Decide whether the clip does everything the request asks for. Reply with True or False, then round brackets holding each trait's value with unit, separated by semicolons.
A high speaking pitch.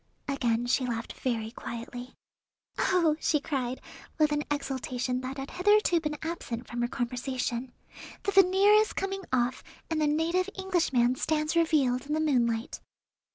True (275 Hz)